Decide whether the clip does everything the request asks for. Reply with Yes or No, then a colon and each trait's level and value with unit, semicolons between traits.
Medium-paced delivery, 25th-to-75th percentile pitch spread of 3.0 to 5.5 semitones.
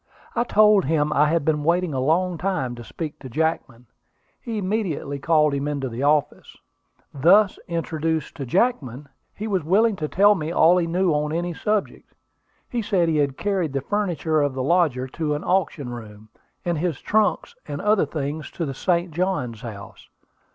Yes: average, 180 wpm; average, 4.6 semitones